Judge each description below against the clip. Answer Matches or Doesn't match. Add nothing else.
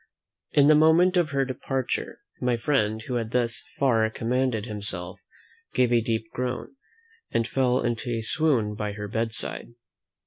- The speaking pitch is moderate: Doesn't match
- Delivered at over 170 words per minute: Doesn't match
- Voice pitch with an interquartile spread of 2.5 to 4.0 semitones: Matches